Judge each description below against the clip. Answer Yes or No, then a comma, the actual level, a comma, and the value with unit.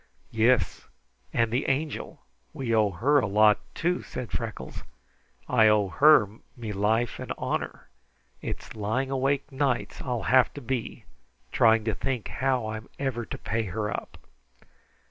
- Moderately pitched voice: No, low, 115 Hz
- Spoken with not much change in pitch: No, average, 3.6 semitones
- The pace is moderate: Yes, average, 145 wpm